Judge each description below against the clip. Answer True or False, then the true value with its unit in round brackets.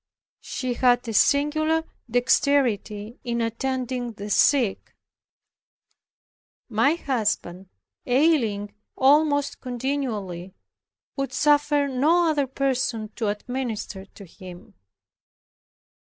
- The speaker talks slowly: True (85 wpm)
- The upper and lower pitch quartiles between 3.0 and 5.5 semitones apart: True (4.9 semitones)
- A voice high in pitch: True (250 Hz)